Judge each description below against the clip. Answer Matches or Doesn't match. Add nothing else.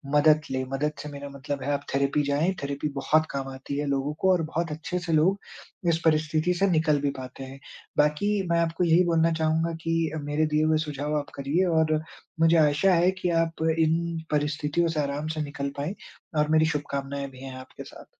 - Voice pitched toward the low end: Doesn't match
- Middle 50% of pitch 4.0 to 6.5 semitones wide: Doesn't match